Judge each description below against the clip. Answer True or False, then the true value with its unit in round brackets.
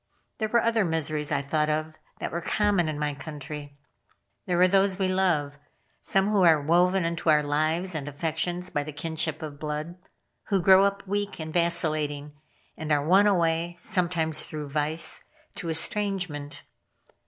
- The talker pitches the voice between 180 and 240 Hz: False (160 Hz)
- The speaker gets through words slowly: False (165 wpm)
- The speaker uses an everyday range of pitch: True (3.5 semitones)